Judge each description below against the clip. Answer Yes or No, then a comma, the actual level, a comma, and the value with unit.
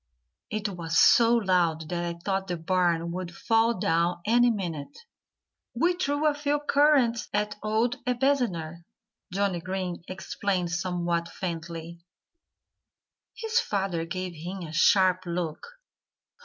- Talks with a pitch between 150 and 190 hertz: Yes, medium, 185 Hz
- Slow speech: Yes, slow, 125 wpm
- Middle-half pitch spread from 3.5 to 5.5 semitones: Yes, average, 5.1 semitones